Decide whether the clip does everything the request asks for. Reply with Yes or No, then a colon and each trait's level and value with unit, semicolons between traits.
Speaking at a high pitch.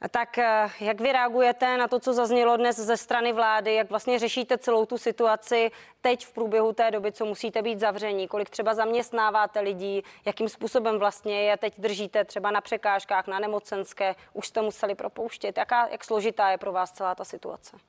Yes: high, 220 Hz